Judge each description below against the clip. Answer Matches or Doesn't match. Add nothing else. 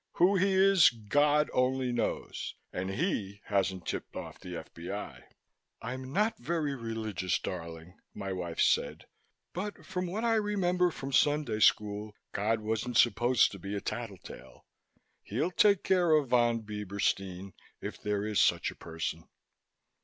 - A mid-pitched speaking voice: Doesn't match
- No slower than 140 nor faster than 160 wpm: Matches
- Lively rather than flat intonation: Matches